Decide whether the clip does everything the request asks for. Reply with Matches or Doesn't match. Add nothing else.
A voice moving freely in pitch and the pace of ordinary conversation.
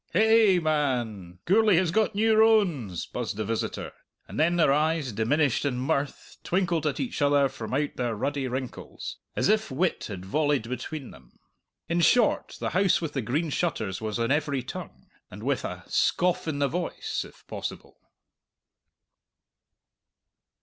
Matches